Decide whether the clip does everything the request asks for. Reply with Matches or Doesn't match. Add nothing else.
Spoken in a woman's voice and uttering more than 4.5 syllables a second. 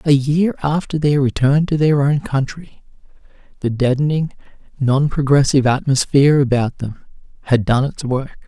Doesn't match